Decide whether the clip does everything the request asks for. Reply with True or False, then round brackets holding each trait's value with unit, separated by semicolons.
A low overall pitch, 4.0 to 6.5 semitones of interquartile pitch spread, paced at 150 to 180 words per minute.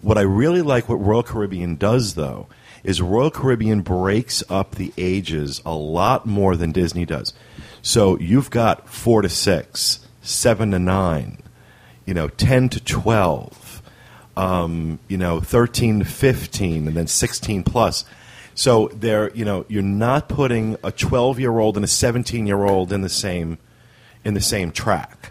True (105 Hz; 4.5 semitones; 165 wpm)